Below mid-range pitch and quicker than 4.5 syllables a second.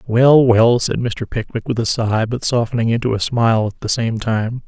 Yes: low, 115 Hz; 5.0 syllables/s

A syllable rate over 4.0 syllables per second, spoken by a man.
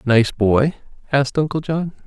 Yes: 4.8 syllables/s; male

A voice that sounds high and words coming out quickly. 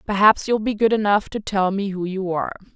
Yes: high, 200 Hz; fast, 240 wpm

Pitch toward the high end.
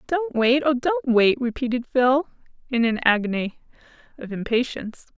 Yes: very high, 250 Hz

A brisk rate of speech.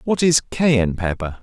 No: average, 170 wpm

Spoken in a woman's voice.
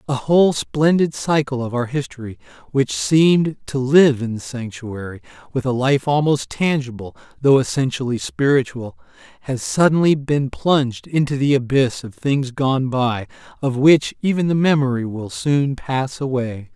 No: male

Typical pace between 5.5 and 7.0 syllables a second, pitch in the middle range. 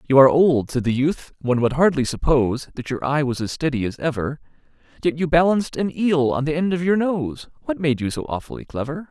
Yes: 6.0 syllables/s; medium, 145 Hz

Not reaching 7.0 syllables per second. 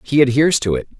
No: 7.4 syllables/s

